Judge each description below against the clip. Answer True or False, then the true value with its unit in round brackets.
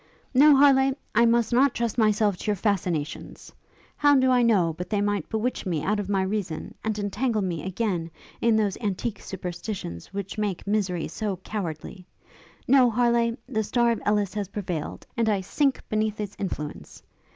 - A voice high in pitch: True (210 Hz)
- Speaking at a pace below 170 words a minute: False (175 wpm)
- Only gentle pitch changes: False (3.7 semitones)